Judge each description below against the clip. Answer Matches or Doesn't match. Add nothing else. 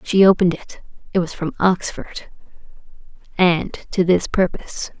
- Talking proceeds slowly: Matches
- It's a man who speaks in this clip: Doesn't match